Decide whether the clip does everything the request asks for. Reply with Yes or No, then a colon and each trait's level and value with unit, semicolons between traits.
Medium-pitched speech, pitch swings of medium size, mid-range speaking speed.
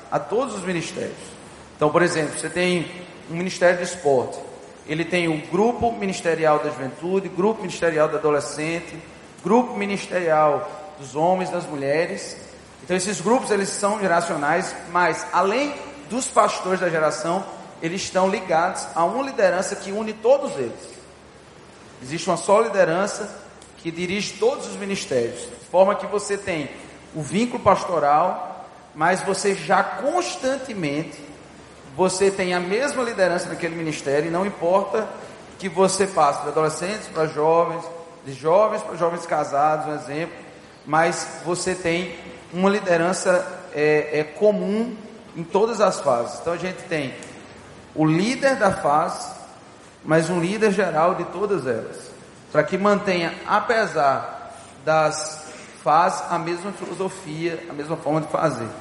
Yes: medium, 180 Hz; average, 4.0 semitones; average, 140 wpm